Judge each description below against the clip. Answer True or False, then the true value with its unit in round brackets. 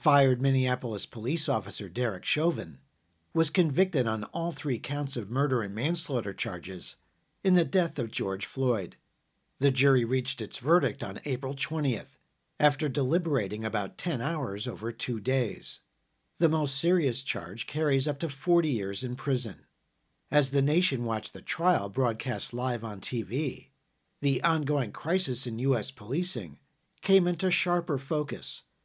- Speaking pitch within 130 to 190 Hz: True (135 Hz)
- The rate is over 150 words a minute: False (145 wpm)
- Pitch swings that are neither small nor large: True (4.9 semitones)